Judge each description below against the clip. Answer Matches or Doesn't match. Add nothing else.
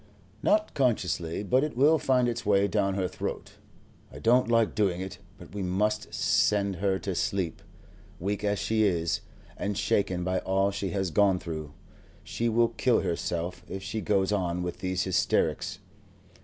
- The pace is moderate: Matches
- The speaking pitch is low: Matches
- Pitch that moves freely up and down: Doesn't match